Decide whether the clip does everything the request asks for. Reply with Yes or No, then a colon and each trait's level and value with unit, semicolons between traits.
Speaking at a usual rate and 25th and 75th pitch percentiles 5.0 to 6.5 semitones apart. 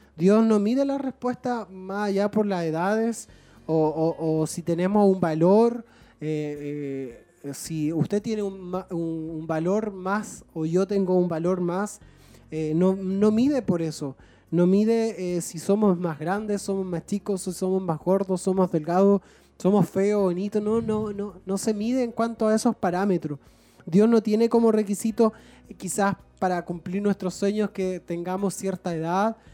No: average, 170 wpm; average, 3.7 semitones